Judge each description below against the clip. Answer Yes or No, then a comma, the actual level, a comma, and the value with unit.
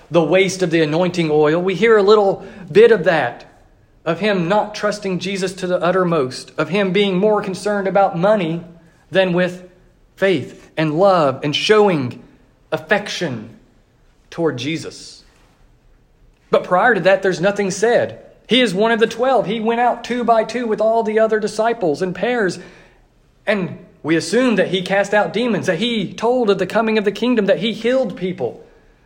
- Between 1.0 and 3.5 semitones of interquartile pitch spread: No, average, 4.1 semitones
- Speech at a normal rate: Yes, average, 175 wpm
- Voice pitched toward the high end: Yes, high, 195 Hz